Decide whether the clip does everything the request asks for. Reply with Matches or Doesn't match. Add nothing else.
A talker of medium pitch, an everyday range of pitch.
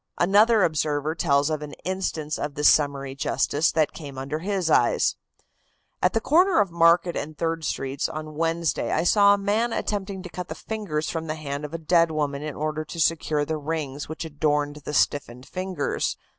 Matches